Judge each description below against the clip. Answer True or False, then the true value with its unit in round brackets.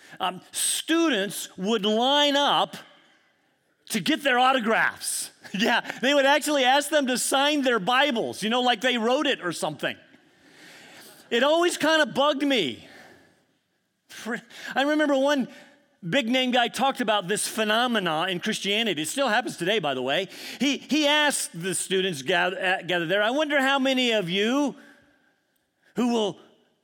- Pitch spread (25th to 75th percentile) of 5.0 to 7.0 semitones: True (5.6 semitones)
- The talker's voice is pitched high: True (250 Hz)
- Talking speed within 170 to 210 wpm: False (155 wpm)